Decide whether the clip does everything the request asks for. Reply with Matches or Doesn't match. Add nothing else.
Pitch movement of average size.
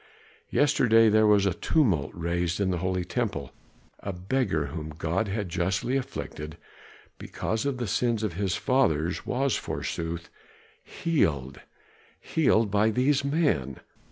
Doesn't match